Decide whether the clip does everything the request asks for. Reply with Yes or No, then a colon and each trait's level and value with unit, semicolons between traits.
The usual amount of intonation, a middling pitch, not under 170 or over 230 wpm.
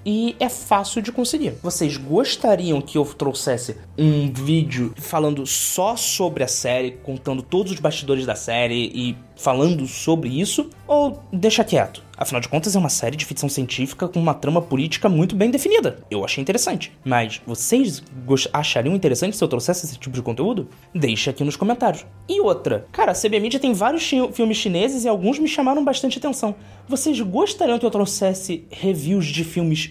No: wide, 8.6 semitones; medium, 170 Hz; average, 175 wpm